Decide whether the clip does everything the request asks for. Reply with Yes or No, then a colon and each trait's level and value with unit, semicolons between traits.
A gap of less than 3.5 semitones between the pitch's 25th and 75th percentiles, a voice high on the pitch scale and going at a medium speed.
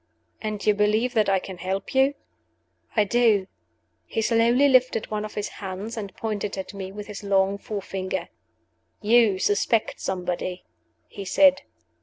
Yes: average, 2.8 semitones; high, 210 Hz; average, 150 wpm